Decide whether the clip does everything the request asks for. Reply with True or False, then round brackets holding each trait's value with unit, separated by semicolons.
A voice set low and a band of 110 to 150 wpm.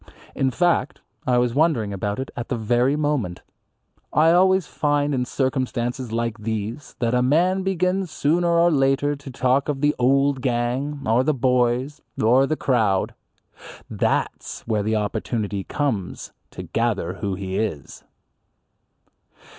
True (130 Hz; 145 wpm)